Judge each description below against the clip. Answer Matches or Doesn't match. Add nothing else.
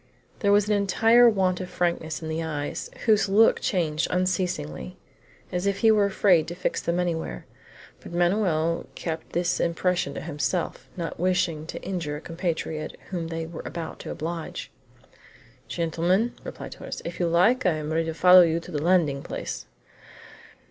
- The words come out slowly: Doesn't match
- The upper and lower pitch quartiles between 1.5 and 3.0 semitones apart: Matches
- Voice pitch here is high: Doesn't match